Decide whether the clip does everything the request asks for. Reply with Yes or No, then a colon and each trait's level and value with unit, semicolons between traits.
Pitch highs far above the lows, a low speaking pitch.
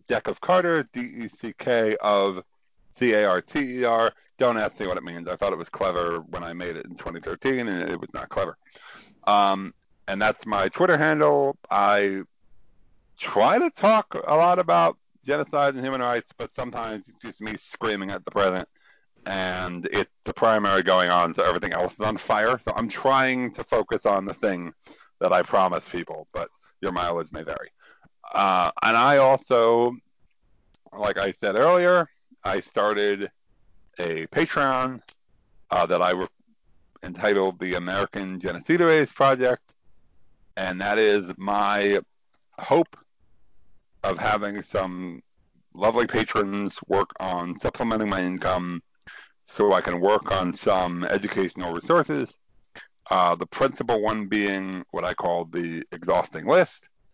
Yes: wide, 6.2 semitones; low, 105 Hz